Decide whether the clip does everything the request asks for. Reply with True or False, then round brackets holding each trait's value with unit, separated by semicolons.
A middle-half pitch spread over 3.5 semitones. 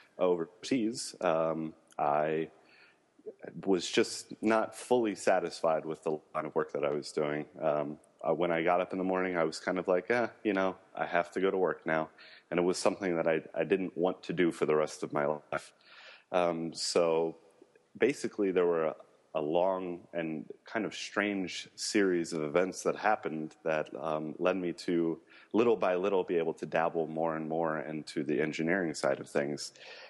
False (2.7 semitones)